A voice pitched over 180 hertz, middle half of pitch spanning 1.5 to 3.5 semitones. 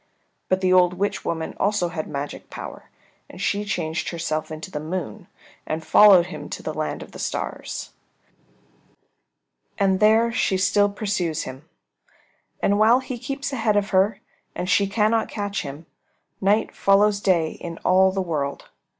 No: high, 190 Hz; average, 3.9 semitones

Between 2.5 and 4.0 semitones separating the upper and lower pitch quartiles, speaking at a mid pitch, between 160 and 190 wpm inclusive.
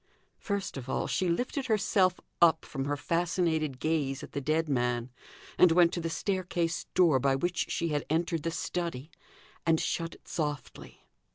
Yes: average, 3.4 semitones; medium, 165 Hz; average, 170 wpm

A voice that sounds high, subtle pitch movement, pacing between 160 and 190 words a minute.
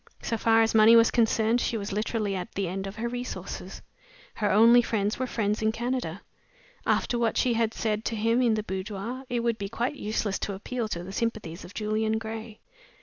No: high, 220 Hz; narrow, 2.2 semitones; fast, 205 wpm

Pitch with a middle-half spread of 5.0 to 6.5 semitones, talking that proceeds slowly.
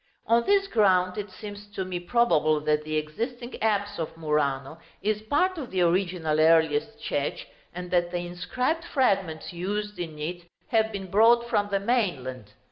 No: wide, 5.4 semitones; average, 165 wpm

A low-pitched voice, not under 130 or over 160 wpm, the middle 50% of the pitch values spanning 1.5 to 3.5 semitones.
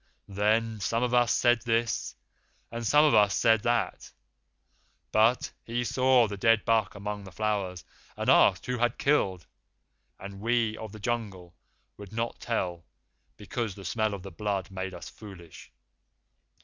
Yes: low, 110 Hz; average, 155 wpm; average, 3.1 semitones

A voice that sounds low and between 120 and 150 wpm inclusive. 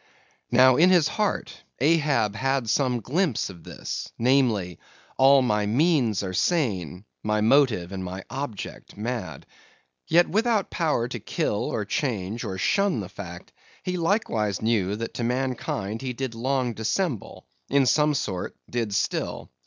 Yes: low, 120 Hz; average, 145 wpm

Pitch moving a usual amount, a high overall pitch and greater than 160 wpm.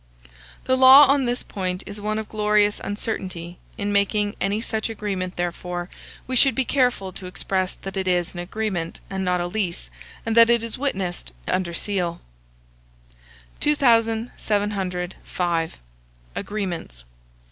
No: average, 3.7 semitones; high, 200 Hz; average, 140 wpm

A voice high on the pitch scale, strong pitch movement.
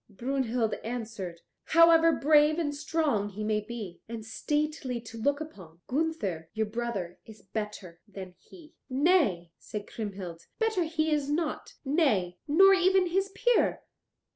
Yes: high, 245 Hz; wide, 7.3 semitones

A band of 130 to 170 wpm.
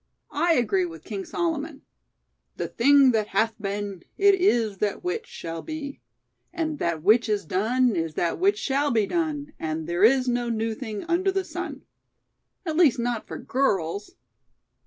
Yes: average, 165 wpm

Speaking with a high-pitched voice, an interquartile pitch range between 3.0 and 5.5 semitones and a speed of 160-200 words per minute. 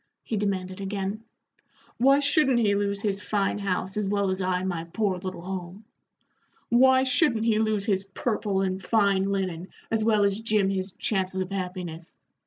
No: high, 200 Hz; narrow, 2.5 semitones; average, 170 wpm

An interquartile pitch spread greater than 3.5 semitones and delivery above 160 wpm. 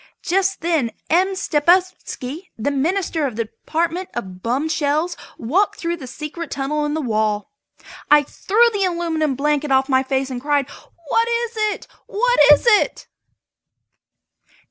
No: average, 5.2 semitones; average, 150 wpm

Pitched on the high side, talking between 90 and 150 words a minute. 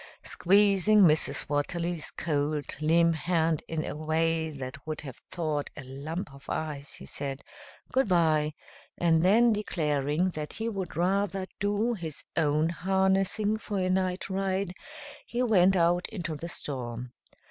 No: medium, 170 Hz; average, 140 wpm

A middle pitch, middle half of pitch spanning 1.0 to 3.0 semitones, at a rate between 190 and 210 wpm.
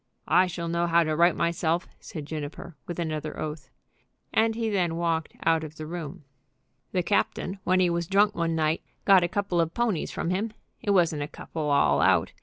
Yes: medium, 170 Hz; average, 2.7 semitones; average, 200 wpm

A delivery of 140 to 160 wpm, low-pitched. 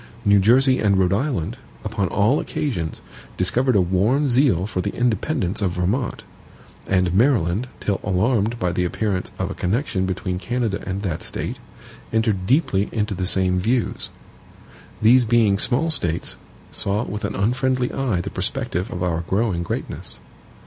Yes: average, 155 wpm; low, 100 Hz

